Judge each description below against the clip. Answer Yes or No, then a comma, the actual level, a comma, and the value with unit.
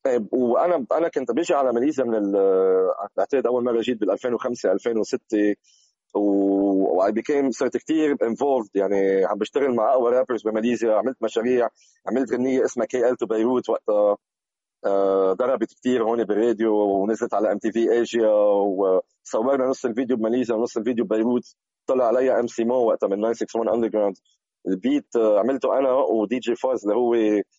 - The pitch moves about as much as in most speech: Yes, average, 3.6 semitones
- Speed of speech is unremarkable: No, fast, 155 wpm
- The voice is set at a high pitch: No, low, 115 Hz